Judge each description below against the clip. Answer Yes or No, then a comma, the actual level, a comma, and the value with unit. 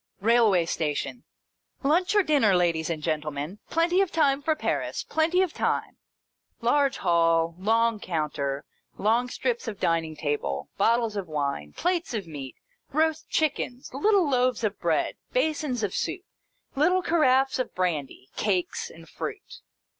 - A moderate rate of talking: Yes, average, 145 wpm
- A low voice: No, high, 230 Hz